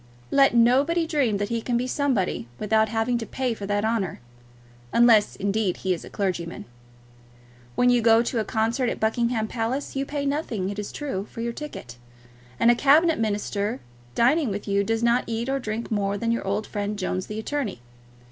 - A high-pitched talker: Yes, high, 225 Hz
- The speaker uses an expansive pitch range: No, average, 3.4 semitones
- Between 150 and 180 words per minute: No, average, 195 wpm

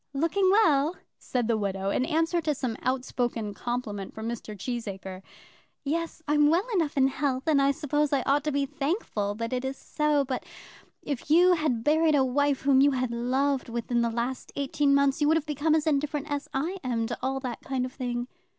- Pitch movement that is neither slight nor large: Yes, average, 3.6 semitones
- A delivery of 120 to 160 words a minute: No, fast, 205 wpm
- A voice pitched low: No, very high, 275 Hz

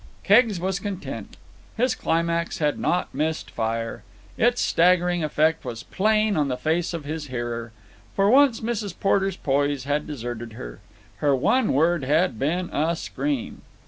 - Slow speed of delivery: No, average, 150 wpm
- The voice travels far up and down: Yes, wide, 5.9 semitones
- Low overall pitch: No, medium, 165 Hz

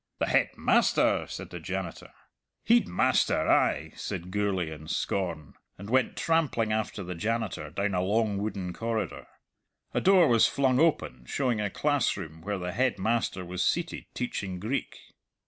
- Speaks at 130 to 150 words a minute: Yes, average, 145 wpm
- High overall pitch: No, low, 105 Hz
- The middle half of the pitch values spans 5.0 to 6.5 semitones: Yes, average, 5.3 semitones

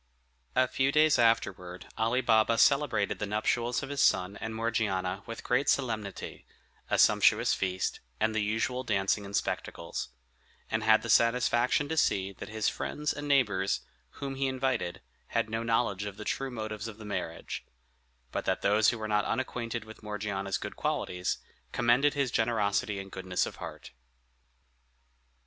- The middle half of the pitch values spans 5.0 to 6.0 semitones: No, average, 3.6 semitones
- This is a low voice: Yes, low, 110 Hz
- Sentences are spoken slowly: No, average, 160 wpm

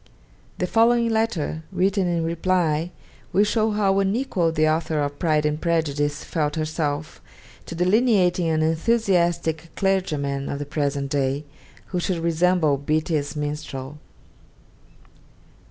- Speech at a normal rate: No, slow, 125 wpm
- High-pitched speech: No, medium, 165 Hz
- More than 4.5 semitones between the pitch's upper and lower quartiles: No, average, 3.7 semitones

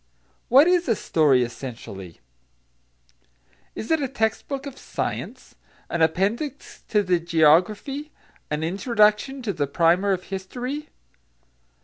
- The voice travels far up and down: Yes, wide, 8.5 semitones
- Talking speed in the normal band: No, slow, 120 wpm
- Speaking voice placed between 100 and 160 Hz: No, high, 200 Hz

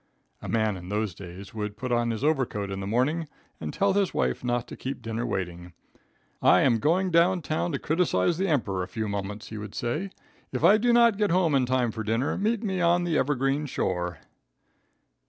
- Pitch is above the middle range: No, low, 125 Hz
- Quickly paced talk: Yes, fast, 210 wpm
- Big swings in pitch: Yes, wide, 8.4 semitones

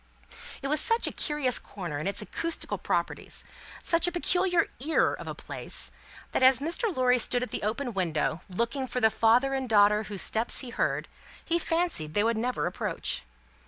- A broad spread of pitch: Yes, wide, 6.1 semitones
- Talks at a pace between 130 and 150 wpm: No, average, 185 wpm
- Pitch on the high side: Yes, very high, 250 Hz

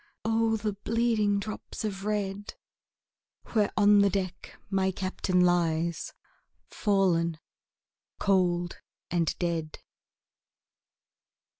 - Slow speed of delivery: Yes, slow, 90 wpm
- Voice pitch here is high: Yes, high, 195 Hz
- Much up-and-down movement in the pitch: No, average, 2.9 semitones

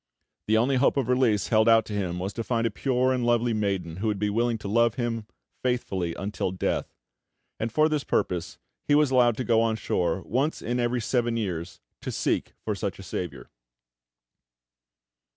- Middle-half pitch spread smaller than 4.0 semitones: Yes, average, 3.4 semitones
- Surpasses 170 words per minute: Yes, average, 190 wpm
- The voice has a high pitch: No, low, 115 Hz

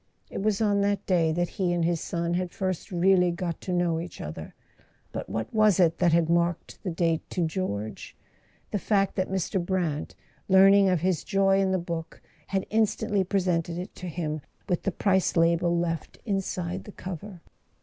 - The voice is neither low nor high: Yes, medium, 180 Hz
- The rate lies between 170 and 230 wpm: Yes, average, 180 wpm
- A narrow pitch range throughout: Yes, narrow, 2.3 semitones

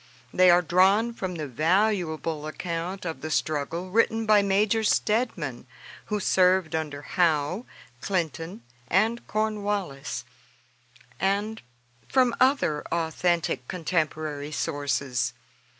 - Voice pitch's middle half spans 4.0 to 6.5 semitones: Yes, average, 5.0 semitones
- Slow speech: Yes, slow, 105 wpm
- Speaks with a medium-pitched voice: Yes, medium, 175 Hz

